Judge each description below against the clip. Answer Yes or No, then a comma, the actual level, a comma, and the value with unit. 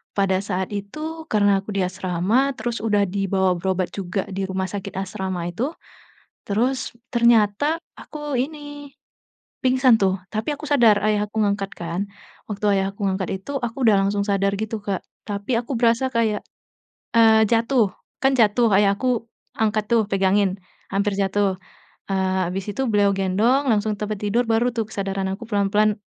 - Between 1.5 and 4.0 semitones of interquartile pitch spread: Yes, average, 3.2 semitones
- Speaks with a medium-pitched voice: No, high, 210 Hz